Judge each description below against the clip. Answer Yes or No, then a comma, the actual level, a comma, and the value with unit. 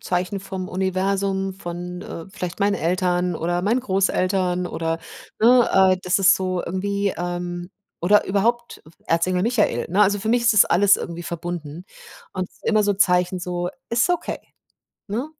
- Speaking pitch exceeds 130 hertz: Yes, medium, 185 Hz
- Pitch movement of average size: No, narrow, 2.2 semitones